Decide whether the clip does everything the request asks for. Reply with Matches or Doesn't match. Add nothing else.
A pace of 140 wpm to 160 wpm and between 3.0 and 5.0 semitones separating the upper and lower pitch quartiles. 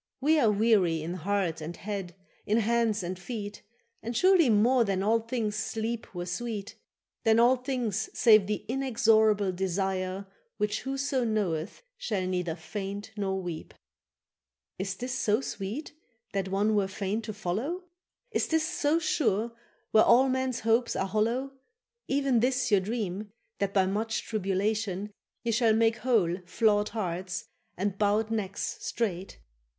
Matches